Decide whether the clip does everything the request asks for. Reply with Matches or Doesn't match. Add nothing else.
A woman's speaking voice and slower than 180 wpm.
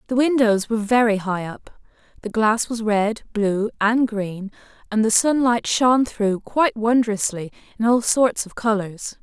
Matches